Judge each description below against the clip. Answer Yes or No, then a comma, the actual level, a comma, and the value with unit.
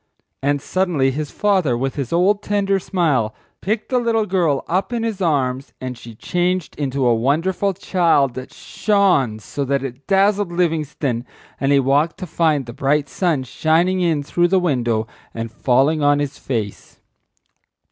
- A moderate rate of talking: Yes, average, 160 wpm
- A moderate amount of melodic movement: No, wide, 5.7 semitones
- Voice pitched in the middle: Yes, medium, 150 Hz